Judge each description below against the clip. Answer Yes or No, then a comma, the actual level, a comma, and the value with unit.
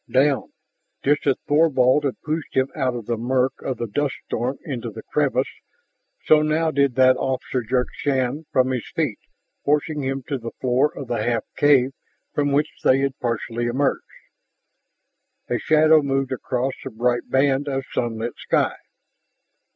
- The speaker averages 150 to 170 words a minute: Yes, average, 160 wpm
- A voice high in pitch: No, low, 135 Hz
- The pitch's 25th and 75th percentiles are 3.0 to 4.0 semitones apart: No, narrow, 2.6 semitones